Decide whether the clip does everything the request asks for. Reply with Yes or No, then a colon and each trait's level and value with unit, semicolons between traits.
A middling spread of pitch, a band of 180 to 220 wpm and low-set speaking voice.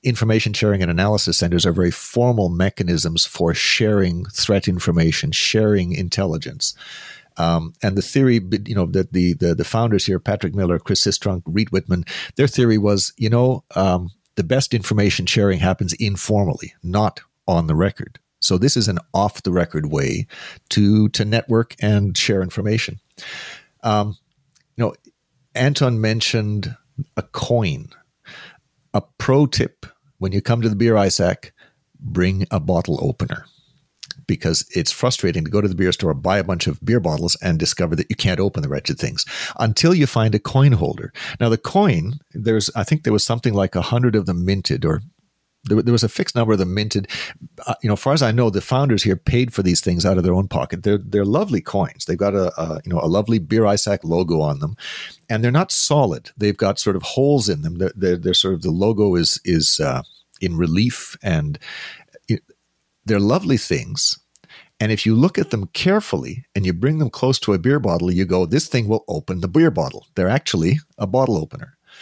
Yes: average, 4.5 semitones; average, 195 wpm; low, 105 Hz